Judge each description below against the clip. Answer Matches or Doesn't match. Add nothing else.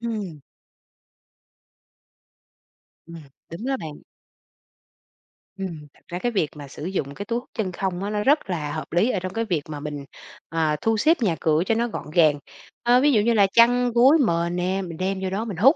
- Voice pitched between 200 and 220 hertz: Doesn't match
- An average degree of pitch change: Doesn't match